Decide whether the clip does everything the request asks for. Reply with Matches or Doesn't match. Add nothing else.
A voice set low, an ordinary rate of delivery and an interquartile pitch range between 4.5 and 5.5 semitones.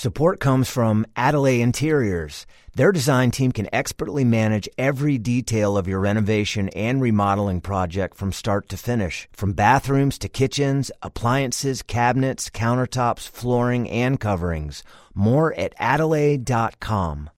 Doesn't match